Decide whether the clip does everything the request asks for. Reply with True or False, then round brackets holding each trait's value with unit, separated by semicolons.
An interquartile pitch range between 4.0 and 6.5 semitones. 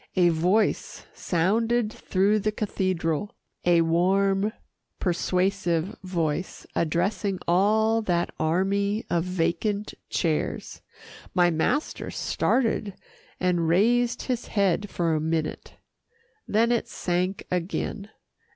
False (3.6 semitones)